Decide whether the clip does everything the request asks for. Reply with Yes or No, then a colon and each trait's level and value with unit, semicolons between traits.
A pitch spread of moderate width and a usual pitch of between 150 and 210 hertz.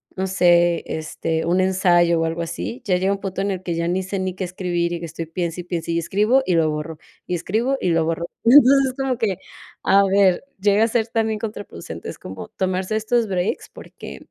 Yes: average, 3.2 semitones; medium, 185 Hz